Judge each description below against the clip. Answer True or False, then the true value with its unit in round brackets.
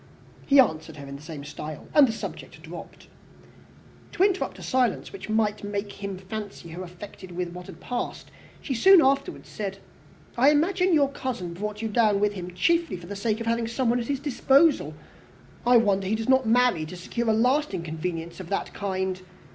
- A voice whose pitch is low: False (215 Hz)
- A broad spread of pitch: True (6.2 semitones)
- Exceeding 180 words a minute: True (195 wpm)